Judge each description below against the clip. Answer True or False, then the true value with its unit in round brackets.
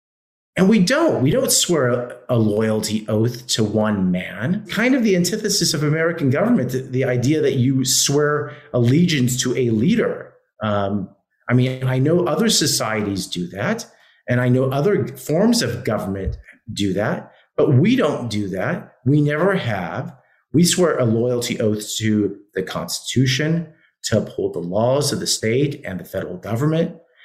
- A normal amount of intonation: False (6.9 semitones)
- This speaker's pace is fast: False (160 wpm)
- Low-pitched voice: True (130 Hz)